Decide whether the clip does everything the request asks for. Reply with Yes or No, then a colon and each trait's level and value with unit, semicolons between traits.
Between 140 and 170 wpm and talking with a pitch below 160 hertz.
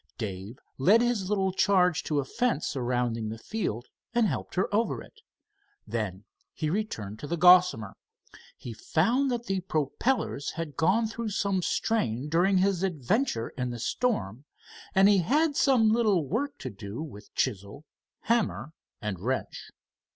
No: average, 150 wpm; medium, 170 Hz